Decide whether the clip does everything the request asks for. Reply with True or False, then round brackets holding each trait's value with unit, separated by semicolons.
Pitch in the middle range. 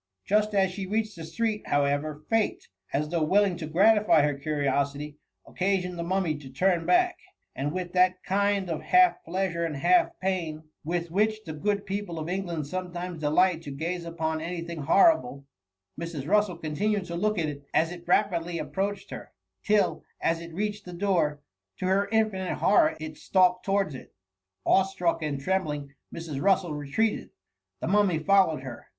True (175 Hz)